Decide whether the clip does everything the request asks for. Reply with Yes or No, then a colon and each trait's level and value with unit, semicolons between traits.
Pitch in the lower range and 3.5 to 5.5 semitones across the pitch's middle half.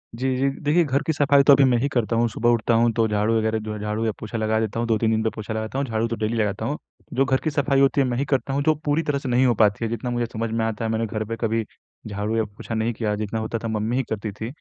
No: low, 115 Hz; average, 3.1 semitones